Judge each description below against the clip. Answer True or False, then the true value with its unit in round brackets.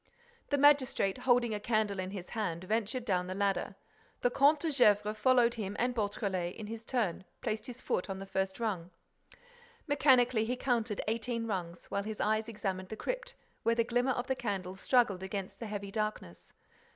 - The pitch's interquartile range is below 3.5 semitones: False (3.9 semitones)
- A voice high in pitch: True (215 Hz)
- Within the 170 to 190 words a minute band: True (185 wpm)